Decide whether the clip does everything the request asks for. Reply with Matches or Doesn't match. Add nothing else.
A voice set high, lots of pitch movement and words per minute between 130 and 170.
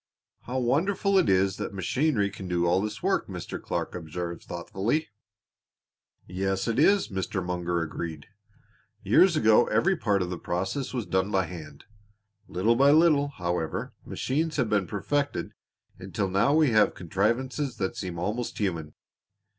Doesn't match